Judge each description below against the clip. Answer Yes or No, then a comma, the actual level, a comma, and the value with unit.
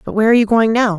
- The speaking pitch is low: No, high, 220 Hz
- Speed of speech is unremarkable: No, fast, 365 wpm